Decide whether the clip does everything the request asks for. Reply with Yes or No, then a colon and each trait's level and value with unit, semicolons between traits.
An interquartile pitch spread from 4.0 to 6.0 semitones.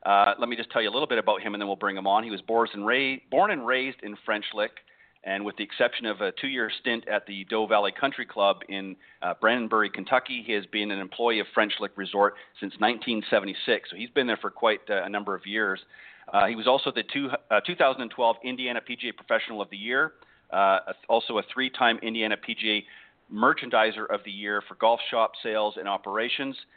No: average, 3.2 semitones